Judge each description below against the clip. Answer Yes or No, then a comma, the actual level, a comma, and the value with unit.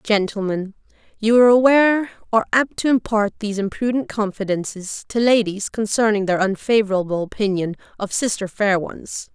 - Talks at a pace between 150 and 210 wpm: No, slow, 135 wpm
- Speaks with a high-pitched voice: Yes, high, 210 Hz